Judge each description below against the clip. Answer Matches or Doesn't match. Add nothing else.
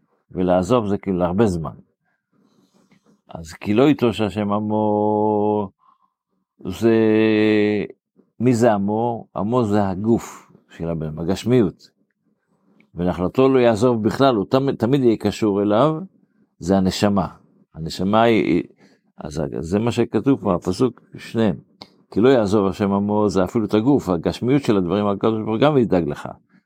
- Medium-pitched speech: Doesn't match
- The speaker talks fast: Doesn't match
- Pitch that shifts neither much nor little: Matches